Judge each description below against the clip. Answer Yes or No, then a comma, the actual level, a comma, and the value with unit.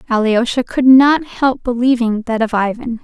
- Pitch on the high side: Yes, high, 240 Hz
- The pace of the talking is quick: No, average, 160 wpm